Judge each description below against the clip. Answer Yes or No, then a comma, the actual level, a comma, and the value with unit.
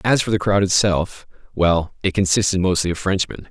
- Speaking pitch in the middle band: No, very low, 95 Hz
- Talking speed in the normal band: Yes, average, 170 wpm